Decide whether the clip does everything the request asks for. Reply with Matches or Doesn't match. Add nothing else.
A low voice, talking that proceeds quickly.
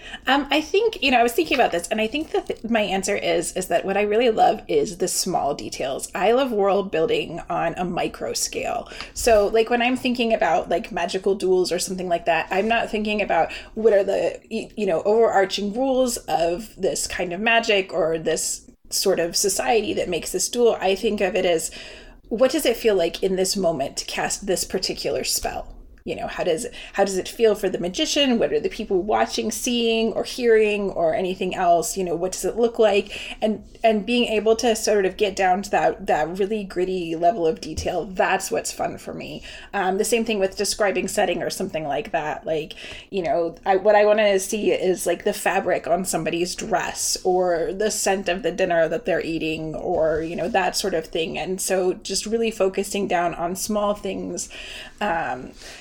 Doesn't match